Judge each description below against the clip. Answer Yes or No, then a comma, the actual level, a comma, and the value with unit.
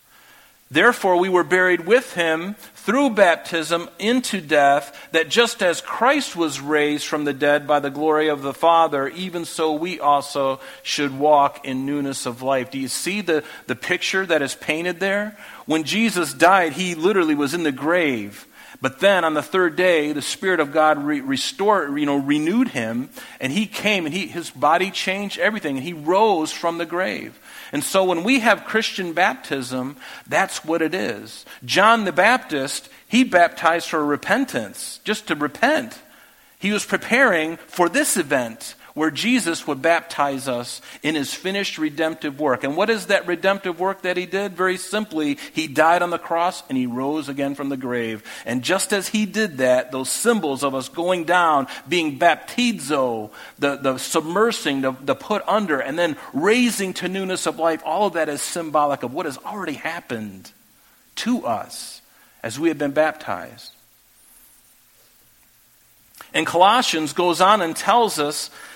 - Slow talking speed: No, average, 170 wpm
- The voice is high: No, medium, 170 Hz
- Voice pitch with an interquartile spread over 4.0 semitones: Yes, average, 5.2 semitones